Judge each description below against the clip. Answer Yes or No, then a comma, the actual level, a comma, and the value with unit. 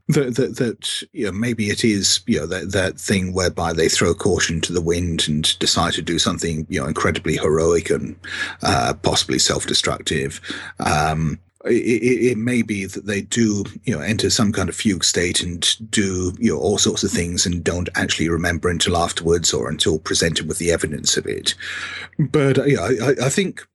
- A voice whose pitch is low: Yes, very low, 95 Hz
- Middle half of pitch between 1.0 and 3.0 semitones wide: No, average, 4.2 semitones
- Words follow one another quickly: No, average, 195 wpm